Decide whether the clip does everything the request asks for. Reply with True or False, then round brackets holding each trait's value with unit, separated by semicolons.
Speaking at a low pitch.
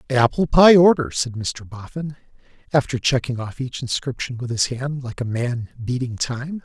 True (130 Hz)